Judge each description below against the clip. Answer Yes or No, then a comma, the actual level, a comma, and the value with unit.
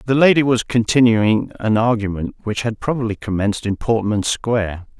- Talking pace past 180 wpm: No, average, 155 wpm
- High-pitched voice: No, low, 110 Hz